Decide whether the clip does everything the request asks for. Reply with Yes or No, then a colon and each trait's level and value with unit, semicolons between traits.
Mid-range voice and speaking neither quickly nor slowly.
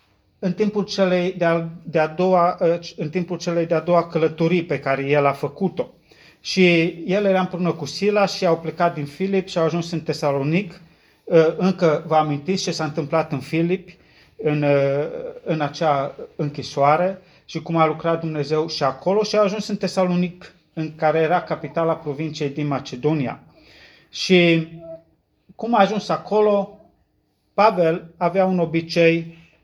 Yes: medium, 165 Hz; average, 150 wpm